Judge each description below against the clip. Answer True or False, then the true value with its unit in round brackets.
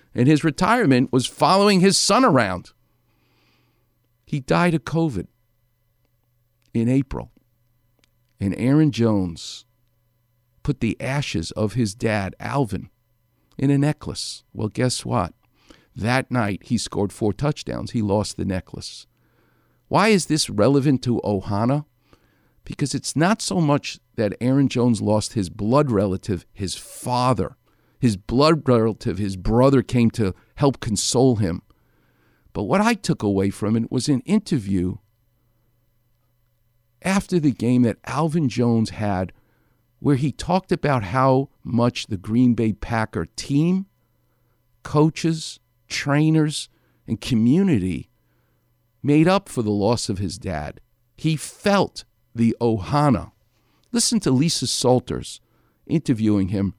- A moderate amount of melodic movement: True (4.4 semitones)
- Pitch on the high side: False (120 Hz)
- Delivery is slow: True (125 wpm)